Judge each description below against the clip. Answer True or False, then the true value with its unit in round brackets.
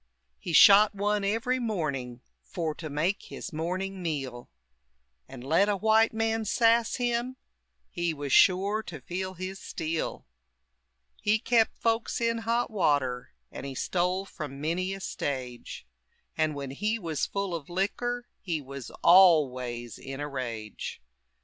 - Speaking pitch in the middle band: True (180 Hz)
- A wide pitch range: True (6.9 semitones)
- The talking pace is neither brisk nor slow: True (145 wpm)